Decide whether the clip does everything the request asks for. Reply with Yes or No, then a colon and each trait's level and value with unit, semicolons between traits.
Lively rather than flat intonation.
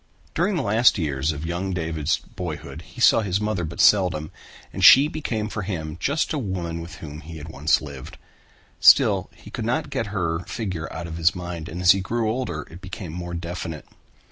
No: average, 4.1 semitones